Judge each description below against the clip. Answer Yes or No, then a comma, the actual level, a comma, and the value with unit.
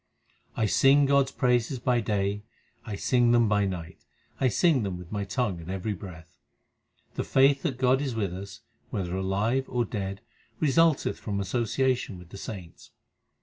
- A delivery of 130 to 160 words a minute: No, average, 175 wpm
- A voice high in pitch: No, low, 110 Hz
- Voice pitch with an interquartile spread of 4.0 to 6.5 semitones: Yes, average, 5.1 semitones